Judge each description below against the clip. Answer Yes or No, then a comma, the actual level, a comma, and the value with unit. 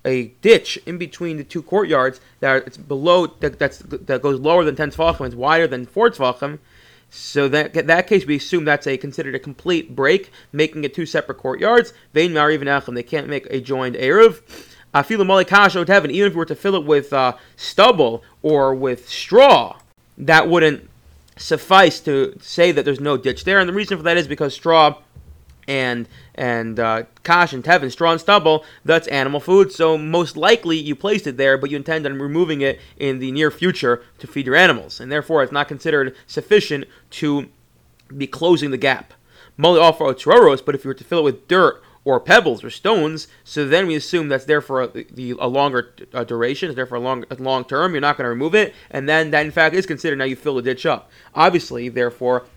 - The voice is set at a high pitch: No, medium, 150 Hz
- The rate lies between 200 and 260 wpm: Yes, fast, 205 wpm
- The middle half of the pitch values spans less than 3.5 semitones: No, average, 4.1 semitones